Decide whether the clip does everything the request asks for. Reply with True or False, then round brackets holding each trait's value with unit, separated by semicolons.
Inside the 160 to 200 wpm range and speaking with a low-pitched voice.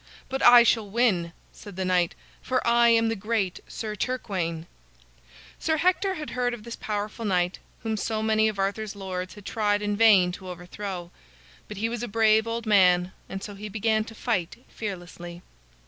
False (180 wpm; 210 Hz)